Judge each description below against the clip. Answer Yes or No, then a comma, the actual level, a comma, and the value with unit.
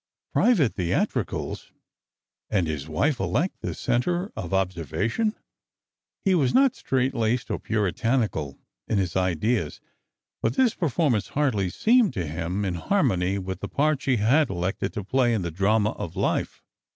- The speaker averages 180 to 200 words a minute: No, average, 150 wpm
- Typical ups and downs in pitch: No, wide, 6.8 semitones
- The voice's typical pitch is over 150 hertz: No, low, 110 Hz